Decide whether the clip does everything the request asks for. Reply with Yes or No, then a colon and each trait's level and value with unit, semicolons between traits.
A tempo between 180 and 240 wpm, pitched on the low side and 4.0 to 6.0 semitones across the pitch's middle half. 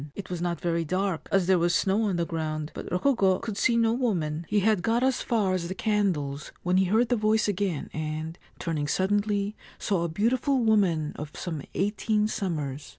No: average, 200 wpm; high, 190 Hz; average, 4.3 semitones